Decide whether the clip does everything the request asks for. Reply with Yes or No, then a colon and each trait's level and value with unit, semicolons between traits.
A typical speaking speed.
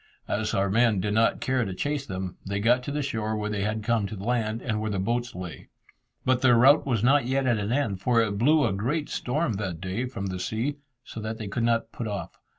No: fast, 250 wpm